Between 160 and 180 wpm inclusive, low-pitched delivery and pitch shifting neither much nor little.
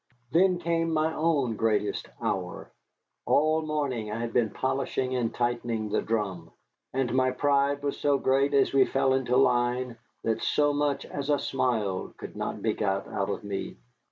Yes: average, 170 wpm; low, 130 Hz; average, 4.0 semitones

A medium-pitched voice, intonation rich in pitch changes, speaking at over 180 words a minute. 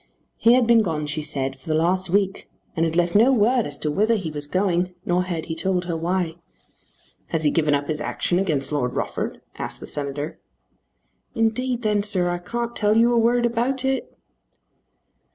Yes: medium, 180 Hz; wide, 6.2 semitones; average, 195 wpm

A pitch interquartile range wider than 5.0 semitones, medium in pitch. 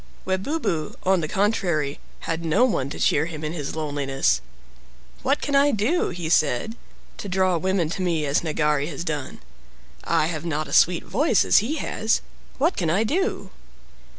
Yes: wide, 5.5 semitones; medium, 170 Hz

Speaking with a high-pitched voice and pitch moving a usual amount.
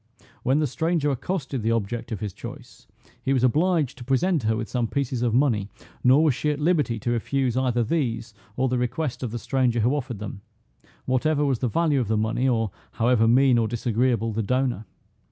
No: low, 125 Hz; average, 3.3 semitones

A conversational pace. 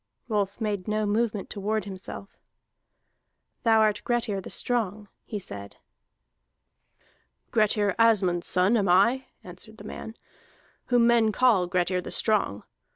No: slow, 130 wpm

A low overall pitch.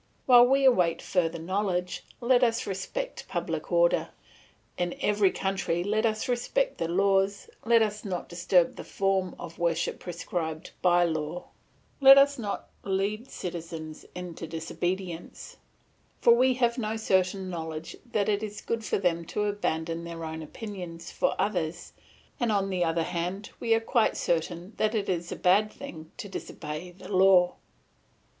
No: high, 190 Hz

